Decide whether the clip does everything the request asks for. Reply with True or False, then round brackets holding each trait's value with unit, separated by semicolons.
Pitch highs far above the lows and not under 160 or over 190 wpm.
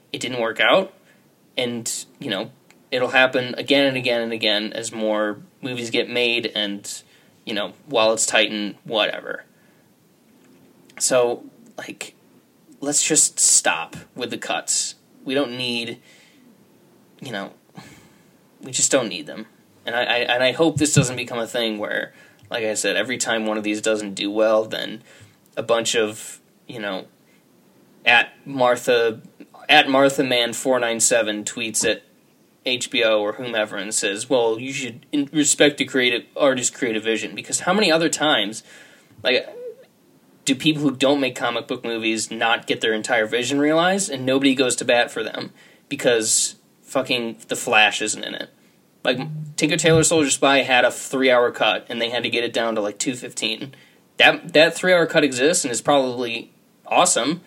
False (3.7 semitones; 165 wpm)